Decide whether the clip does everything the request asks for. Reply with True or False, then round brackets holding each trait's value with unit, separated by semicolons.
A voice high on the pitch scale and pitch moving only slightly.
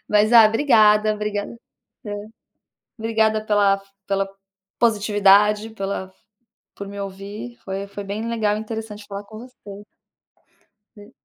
True (210 Hz; 1.5 semitones)